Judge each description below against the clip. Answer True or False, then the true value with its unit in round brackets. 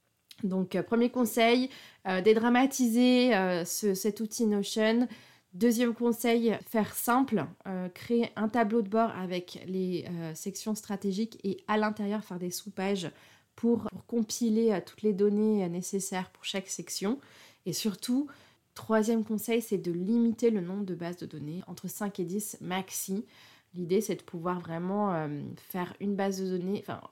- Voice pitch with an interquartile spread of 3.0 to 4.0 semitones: True (3.6 semitones)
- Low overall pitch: False (205 Hz)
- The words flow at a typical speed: True (160 wpm)